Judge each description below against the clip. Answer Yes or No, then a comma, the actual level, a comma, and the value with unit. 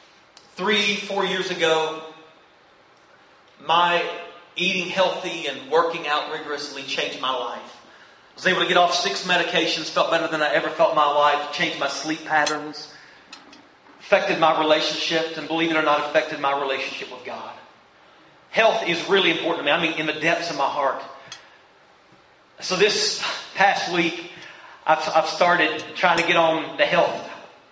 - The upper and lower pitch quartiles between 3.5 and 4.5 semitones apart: No, narrow, 2.5 semitones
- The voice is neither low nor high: Yes, medium, 165 Hz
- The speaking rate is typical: Yes, average, 160 wpm